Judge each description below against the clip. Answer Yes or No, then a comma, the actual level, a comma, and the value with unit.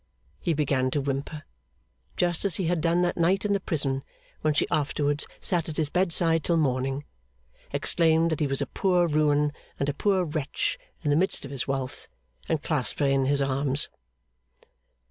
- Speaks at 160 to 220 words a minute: Yes, average, 185 wpm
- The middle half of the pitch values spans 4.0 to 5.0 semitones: No, average, 3.3 semitones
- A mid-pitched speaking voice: Yes, medium, 150 Hz